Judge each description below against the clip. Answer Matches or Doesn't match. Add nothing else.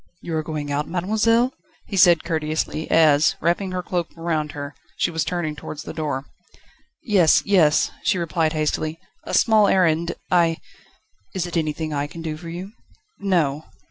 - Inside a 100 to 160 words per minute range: Doesn't match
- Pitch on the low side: Doesn't match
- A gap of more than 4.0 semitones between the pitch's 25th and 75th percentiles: Doesn't match